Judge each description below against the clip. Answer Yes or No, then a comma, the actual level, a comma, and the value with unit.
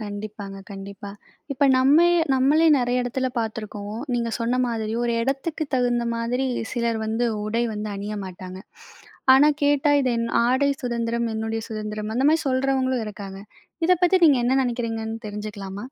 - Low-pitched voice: No, high, 230 Hz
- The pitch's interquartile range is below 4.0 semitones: Yes, average, 3.4 semitones